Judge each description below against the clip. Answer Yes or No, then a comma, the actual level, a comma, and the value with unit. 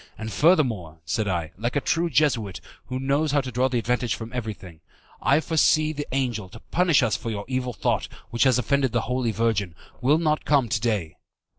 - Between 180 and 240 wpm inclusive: Yes, average, 200 wpm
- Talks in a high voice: No, low, 125 Hz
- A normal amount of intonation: Yes, average, 4.3 semitones